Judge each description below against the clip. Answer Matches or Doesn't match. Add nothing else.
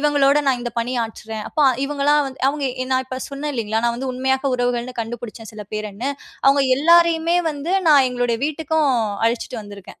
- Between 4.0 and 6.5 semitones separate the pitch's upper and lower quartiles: Doesn't match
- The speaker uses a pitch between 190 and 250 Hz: Doesn't match